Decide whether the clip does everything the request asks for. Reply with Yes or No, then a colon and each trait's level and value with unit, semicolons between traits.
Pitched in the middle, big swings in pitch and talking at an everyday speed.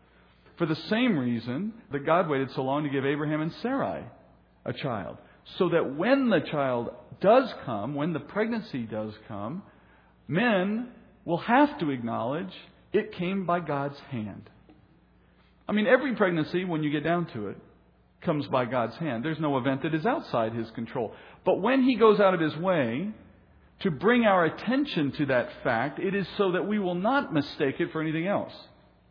Yes: medium, 160 Hz; wide, 7.1 semitones; average, 180 wpm